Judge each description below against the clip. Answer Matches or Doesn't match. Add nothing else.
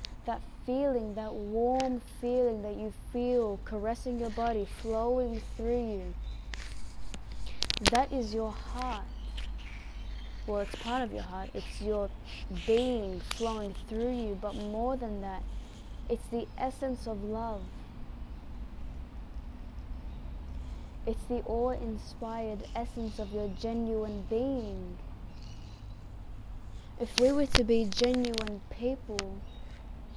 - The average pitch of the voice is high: Matches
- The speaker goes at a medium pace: Doesn't match